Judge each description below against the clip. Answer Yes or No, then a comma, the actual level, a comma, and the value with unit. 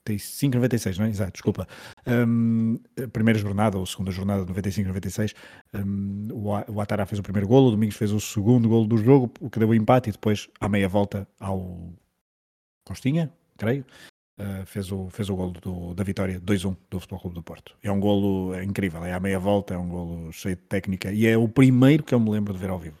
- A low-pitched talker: Yes, low, 100 Hz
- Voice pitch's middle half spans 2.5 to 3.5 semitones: Yes, average, 2.9 semitones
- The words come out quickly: Yes, fast, 215 wpm